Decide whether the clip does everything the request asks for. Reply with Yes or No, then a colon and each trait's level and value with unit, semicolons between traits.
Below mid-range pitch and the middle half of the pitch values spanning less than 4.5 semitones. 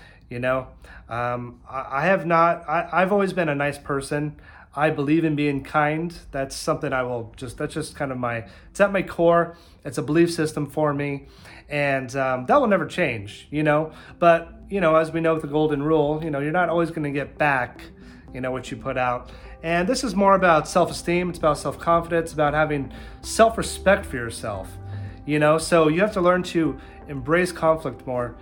No: medium, 150 Hz; average, 4.0 semitones